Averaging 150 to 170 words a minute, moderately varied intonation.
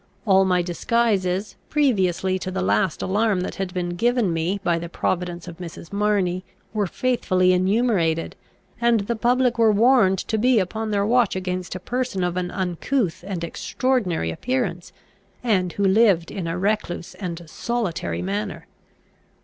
Yes: average, 155 wpm; average, 4.1 semitones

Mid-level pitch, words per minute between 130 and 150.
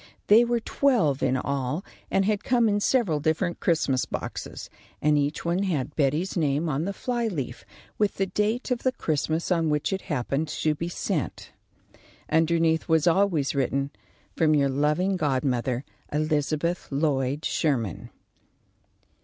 Yes: medium, 160 Hz; average, 145 wpm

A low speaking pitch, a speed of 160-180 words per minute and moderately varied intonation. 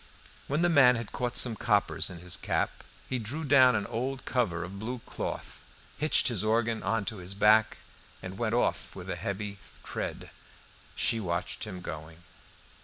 Yes: low, 110 Hz; average, 175 wpm; average, 4.2 semitones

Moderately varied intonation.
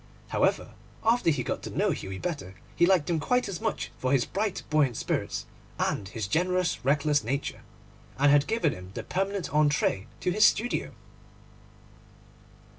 No: wide, 5.9 semitones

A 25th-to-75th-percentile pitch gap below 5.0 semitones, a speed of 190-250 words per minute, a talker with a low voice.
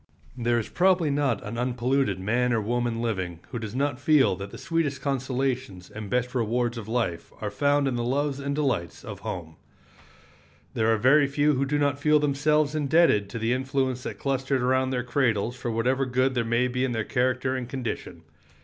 Yes: average, 3.1 semitones; average, 195 wpm; low, 125 Hz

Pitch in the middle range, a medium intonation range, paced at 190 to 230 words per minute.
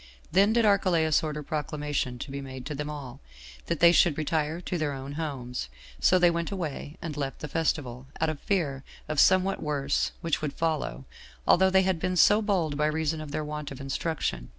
Yes: medium, 155 Hz; average, 3.3 semitones; average, 200 wpm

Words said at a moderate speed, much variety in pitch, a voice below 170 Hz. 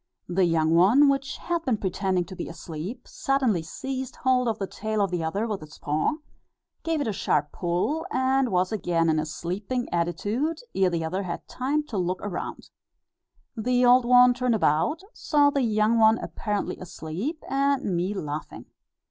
No: average, 175 wpm; wide, 6.7 semitones; high, 210 Hz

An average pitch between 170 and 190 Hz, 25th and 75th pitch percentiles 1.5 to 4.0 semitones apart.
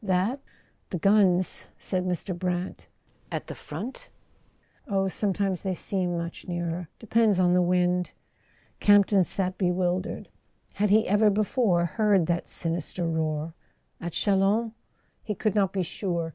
Yes: medium, 185 Hz; narrow, 2.6 semitones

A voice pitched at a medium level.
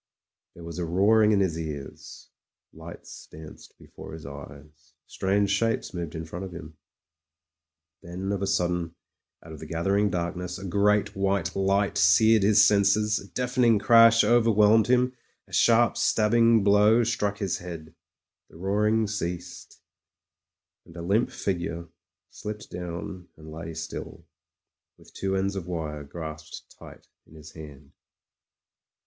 No: very low, 95 Hz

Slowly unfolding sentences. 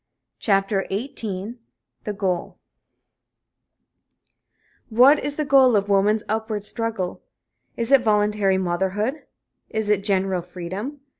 Yes: slow, 105 wpm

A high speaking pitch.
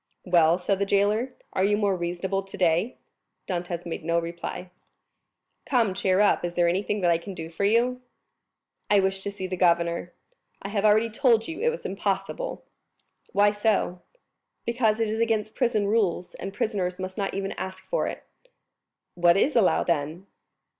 Yes: high, 195 Hz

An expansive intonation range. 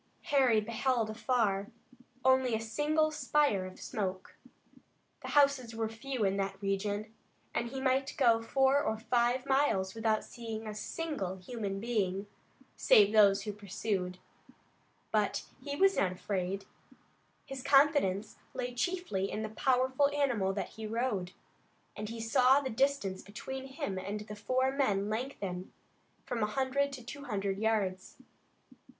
No: average, 4.8 semitones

